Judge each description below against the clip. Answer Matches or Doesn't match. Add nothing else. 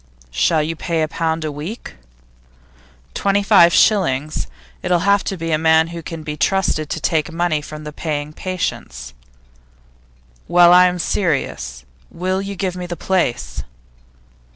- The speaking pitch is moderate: Matches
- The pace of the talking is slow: Doesn't match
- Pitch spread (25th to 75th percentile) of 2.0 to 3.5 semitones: Matches